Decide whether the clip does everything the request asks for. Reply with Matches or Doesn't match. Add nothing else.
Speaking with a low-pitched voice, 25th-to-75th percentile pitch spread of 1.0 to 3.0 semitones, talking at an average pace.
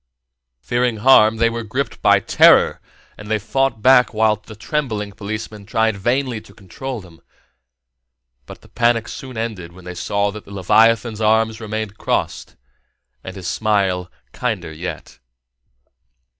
Matches